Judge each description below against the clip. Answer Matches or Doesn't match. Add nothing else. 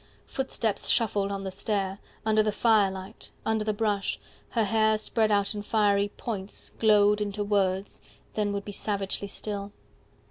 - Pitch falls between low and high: Doesn't match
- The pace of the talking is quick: Doesn't match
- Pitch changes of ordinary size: Doesn't match